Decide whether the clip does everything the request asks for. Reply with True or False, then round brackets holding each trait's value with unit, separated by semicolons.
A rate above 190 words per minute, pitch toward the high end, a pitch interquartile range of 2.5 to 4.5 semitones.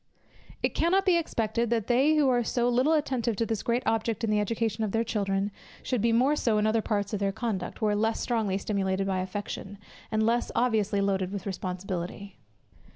True (200 wpm; 220 Hz; 3.2 semitones)